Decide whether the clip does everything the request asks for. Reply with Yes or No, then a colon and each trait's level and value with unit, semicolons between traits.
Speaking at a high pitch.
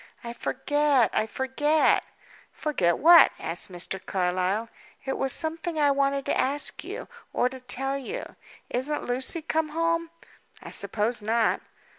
Yes: very high, 270 Hz